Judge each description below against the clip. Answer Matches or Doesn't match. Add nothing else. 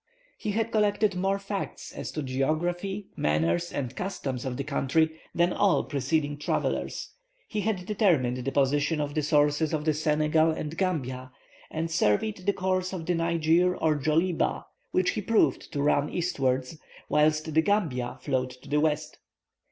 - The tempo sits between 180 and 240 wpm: Doesn't match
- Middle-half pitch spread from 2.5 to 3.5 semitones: Doesn't match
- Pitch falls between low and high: Matches